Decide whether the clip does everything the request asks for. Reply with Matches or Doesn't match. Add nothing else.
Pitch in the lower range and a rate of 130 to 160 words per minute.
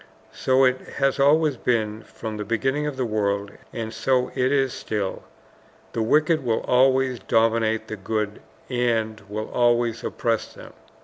Matches